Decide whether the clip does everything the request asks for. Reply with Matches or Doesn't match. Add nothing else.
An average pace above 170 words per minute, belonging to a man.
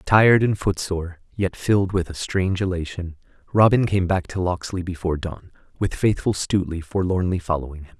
Doesn't match